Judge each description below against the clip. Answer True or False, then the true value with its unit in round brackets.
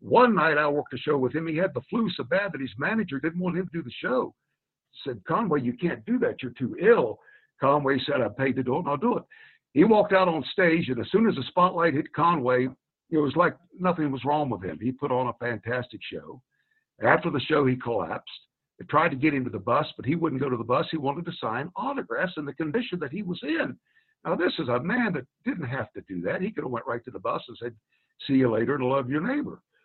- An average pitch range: False (6.2 semitones)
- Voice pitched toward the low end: False (150 Hz)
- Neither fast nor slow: False (265 wpm)